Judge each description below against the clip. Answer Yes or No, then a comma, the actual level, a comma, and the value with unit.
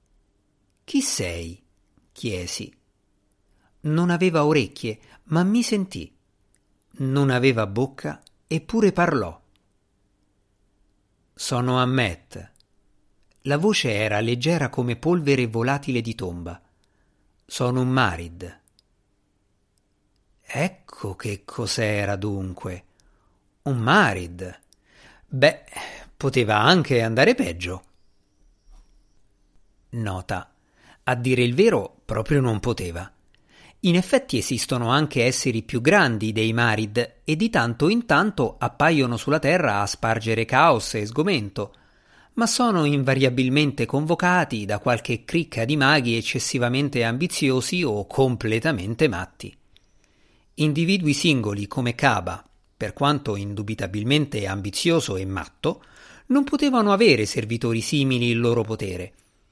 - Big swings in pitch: Yes, wide, 5.8 semitones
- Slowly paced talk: Yes, slow, 100 wpm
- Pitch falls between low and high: No, low, 115 Hz